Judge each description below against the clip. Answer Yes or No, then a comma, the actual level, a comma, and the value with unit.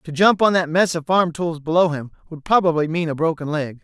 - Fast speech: Yes, fast, 250 wpm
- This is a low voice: No, medium, 165 Hz